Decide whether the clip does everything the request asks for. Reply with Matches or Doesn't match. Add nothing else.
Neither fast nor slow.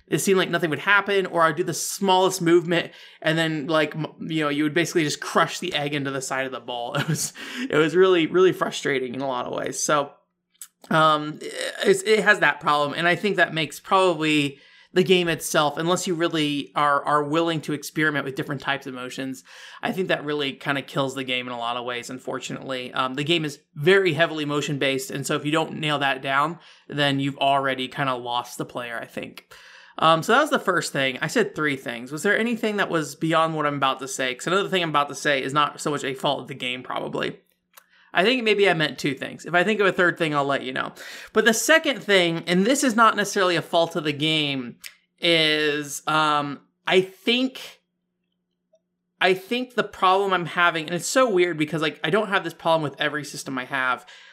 Doesn't match